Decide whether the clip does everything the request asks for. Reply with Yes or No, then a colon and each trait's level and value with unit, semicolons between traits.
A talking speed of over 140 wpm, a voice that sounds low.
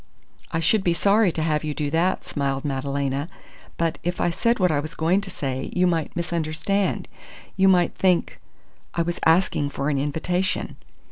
No: average, 180 wpm; medium, 165 Hz